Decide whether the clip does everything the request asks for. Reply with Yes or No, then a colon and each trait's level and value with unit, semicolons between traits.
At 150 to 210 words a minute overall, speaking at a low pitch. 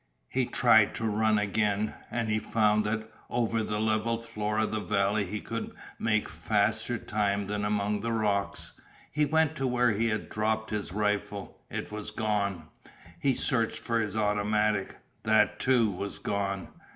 Yes: average, 165 wpm; low, 105 Hz